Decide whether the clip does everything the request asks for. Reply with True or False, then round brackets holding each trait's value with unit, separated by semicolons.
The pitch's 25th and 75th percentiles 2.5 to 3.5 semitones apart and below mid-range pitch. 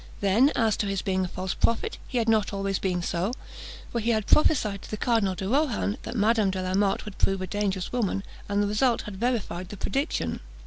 False (3.2 semitones; 205 Hz)